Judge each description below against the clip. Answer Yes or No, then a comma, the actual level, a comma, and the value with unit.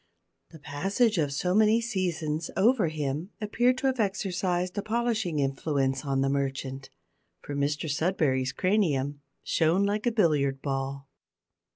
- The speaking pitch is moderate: Yes, medium, 160 Hz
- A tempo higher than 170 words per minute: No, average, 140 wpm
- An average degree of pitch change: No, wide, 6.5 semitones